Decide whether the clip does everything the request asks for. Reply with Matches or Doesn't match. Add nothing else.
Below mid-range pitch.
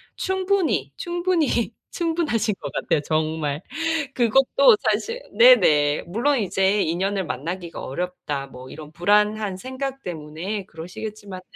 Doesn't match